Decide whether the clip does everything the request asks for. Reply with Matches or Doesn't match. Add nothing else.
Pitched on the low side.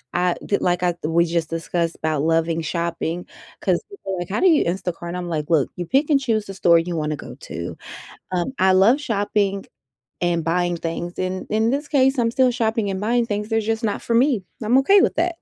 Doesn't match